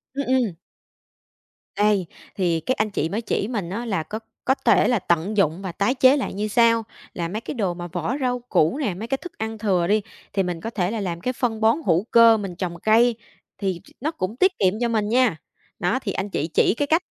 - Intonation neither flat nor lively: Yes, average, 4.7 semitones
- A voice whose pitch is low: No, high, 210 Hz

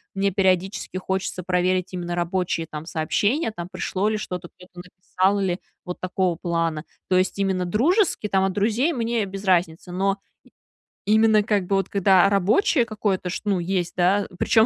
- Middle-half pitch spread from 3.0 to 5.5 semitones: No, narrow, 2.4 semitones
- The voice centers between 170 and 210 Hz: Yes, high, 190 Hz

